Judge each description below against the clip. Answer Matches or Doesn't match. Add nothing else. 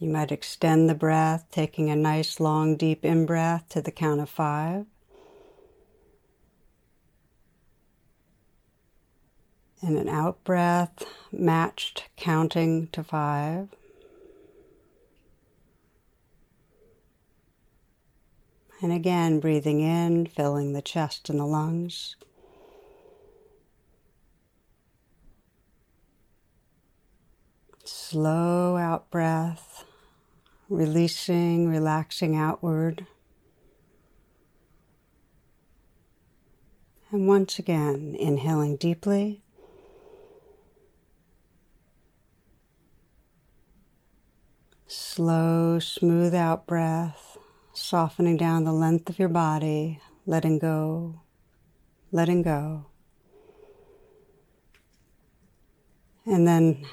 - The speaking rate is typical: Doesn't match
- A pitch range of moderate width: Matches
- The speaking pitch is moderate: Matches